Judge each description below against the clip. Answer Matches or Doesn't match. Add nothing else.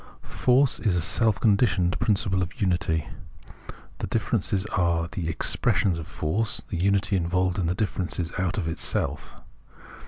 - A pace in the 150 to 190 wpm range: Doesn't match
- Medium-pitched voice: Doesn't match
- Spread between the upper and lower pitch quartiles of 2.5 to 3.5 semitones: Matches